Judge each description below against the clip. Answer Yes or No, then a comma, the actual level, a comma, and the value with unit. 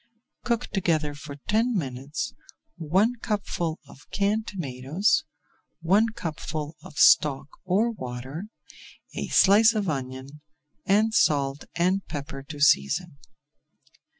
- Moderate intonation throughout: No, wide, 6.6 semitones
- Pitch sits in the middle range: Yes, medium, 165 Hz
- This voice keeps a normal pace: No, slow, 110 wpm